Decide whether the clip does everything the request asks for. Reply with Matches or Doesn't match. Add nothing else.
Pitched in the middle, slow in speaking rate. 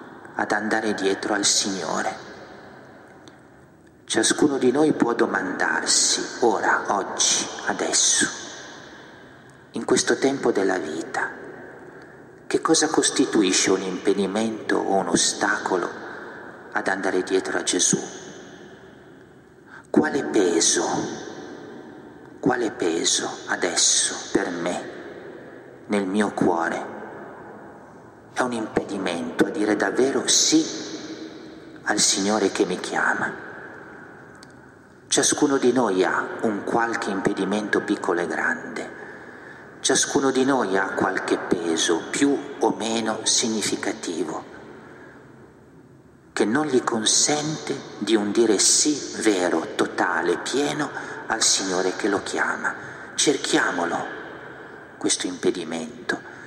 Matches